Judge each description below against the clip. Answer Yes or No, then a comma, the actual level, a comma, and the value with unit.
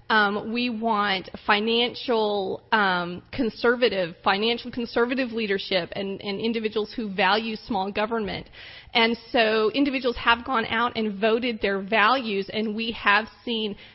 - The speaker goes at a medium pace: No, slow, 125 wpm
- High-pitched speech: Yes, high, 220 Hz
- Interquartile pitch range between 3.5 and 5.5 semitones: No, narrow, 2.4 semitones